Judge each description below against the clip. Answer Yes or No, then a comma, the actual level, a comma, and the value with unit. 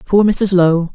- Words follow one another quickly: No, average, 190 wpm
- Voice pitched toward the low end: No, medium, 185 Hz